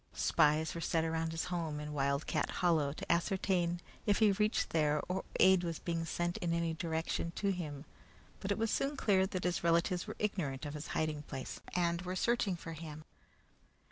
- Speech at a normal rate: Yes, average, 190 wpm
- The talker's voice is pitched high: No, medium, 170 Hz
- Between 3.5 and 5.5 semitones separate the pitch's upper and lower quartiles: No, average, 2.9 semitones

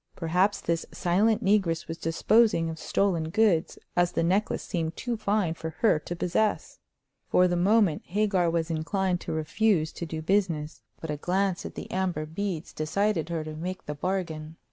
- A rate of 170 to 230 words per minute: Yes, average, 175 wpm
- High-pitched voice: No, medium, 175 Hz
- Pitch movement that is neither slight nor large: Yes, average, 3.6 semitones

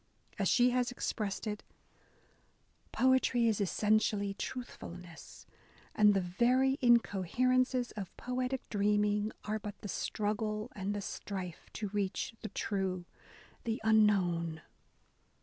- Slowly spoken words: Yes, slow, 115 wpm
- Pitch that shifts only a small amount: No, average, 3.4 semitones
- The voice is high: Yes, high, 210 Hz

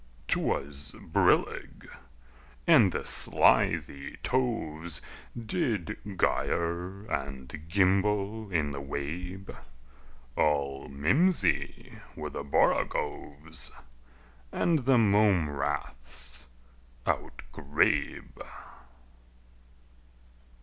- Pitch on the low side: Yes, very low, 80 Hz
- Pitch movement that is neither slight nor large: No, wide, 6.3 semitones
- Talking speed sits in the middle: No, slow, 65 wpm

